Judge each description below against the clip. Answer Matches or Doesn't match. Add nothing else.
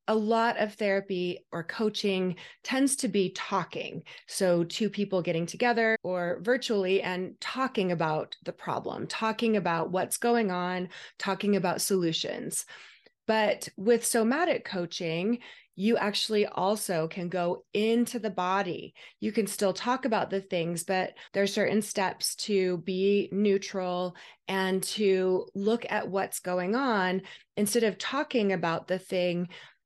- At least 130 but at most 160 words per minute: Matches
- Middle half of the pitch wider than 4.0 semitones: Doesn't match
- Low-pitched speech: Doesn't match